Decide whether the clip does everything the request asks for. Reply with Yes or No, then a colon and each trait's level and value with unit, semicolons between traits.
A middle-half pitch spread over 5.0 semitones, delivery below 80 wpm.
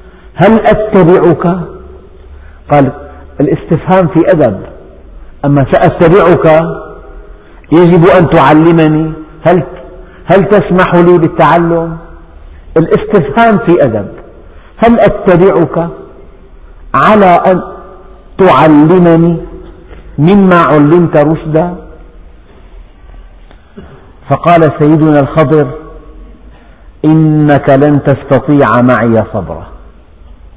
Yes: wide, 5.6 semitones; average, 70 wpm